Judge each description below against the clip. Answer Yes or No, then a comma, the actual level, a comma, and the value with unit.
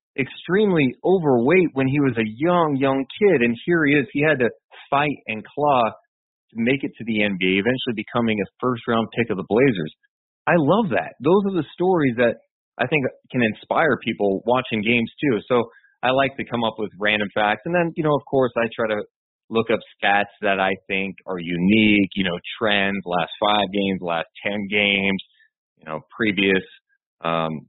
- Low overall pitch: Yes, low, 115 Hz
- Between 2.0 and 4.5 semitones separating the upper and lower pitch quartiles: No, average, 5.2 semitones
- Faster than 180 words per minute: Yes, average, 195 wpm